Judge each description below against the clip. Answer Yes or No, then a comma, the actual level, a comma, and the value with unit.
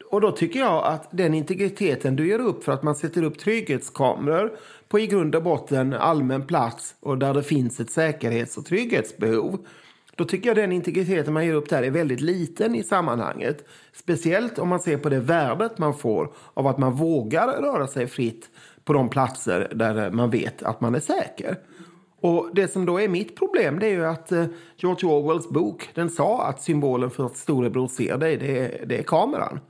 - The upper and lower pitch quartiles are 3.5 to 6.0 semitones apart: Yes, average, 4.6 semitones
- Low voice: No, medium, 160 Hz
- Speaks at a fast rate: Yes, fast, 200 wpm